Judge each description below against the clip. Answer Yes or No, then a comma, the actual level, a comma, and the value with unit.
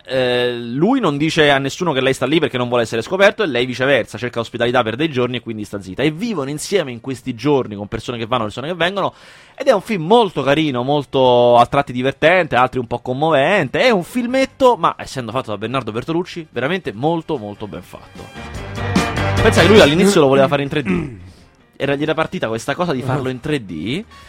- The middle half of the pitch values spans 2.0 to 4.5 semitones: No, average, 4.9 semitones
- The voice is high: No, low, 130 Hz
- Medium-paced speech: No, fast, 215 wpm